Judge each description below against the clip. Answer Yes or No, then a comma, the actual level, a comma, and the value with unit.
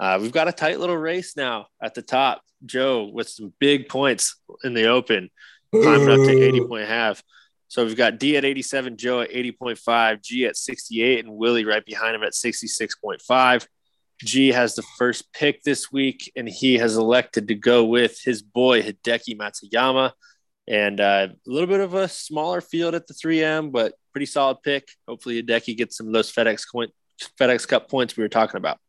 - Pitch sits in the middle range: No, low, 125 Hz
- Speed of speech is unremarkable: Yes, average, 190 wpm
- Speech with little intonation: No, average, 3.5 semitones